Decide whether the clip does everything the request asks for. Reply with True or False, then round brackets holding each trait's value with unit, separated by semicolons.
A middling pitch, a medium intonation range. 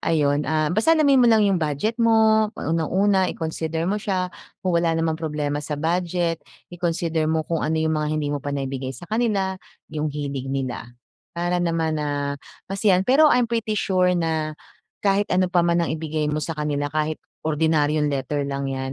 True (160 Hz; 3.9 semitones)